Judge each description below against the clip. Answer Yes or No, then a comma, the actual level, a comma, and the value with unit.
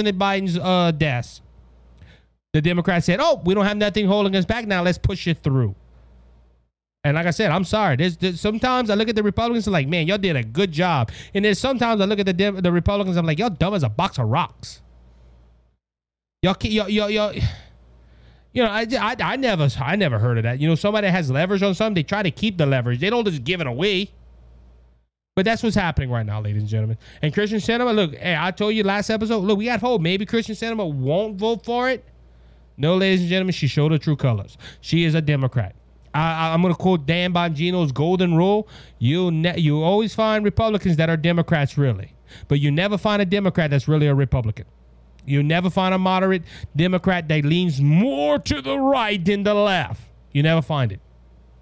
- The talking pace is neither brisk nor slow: No, fast, 220 wpm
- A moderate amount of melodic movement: No, wide, 8.0 semitones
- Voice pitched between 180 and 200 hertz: No, medium, 170 Hz